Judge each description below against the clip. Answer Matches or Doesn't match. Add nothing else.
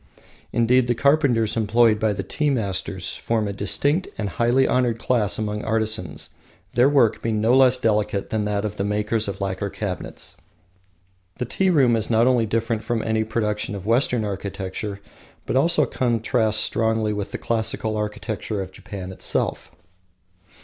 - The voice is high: Doesn't match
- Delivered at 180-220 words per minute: Doesn't match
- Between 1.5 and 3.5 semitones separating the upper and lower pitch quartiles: Matches